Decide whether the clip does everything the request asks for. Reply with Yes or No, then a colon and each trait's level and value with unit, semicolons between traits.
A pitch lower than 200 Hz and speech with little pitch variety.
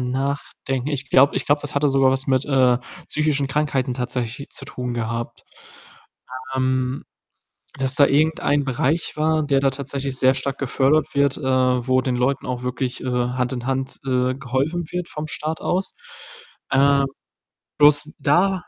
Yes: low, 135 Hz; narrow, 2.1 semitones